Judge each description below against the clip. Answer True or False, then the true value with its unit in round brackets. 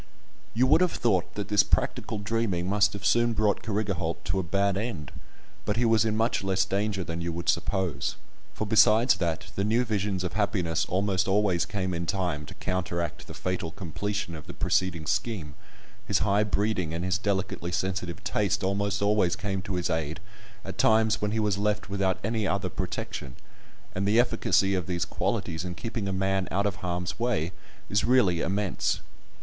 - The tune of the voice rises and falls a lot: False (2.9 semitones)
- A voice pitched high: False (95 Hz)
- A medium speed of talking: True (185 wpm)